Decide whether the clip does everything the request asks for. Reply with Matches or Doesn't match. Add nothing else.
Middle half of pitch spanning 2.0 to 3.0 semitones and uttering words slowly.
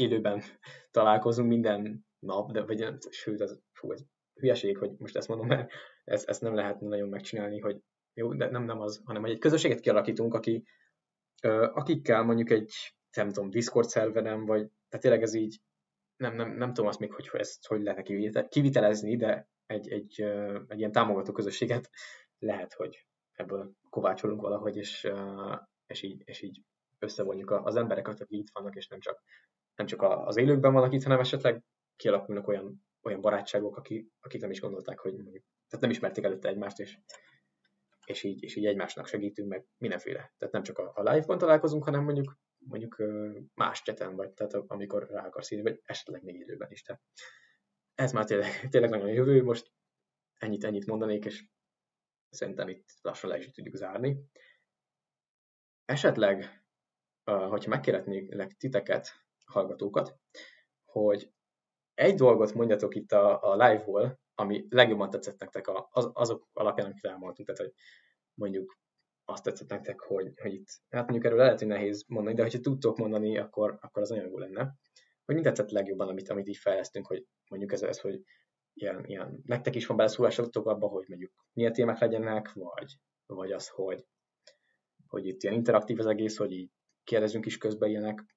Doesn't match